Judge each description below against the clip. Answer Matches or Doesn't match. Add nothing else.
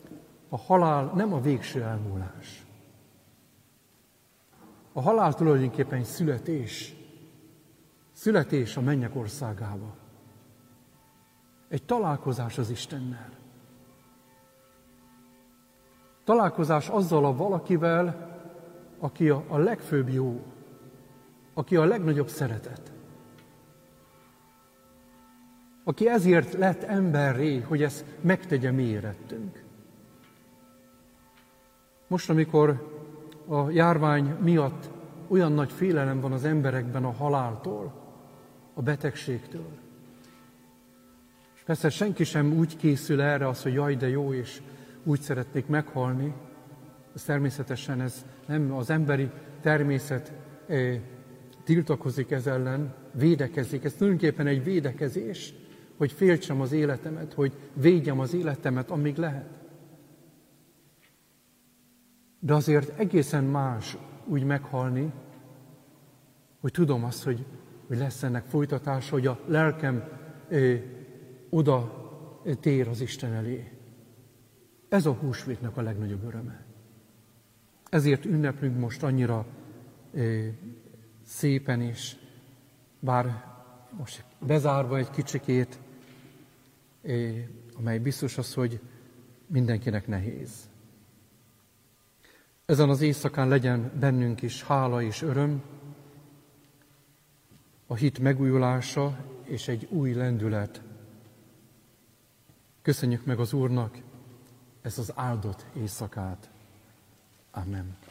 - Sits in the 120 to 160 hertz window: Matches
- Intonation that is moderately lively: Matches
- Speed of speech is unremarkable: Doesn't match